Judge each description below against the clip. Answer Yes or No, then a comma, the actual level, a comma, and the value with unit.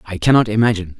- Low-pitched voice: Yes, low, 105 Hz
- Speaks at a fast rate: No, average, 180 wpm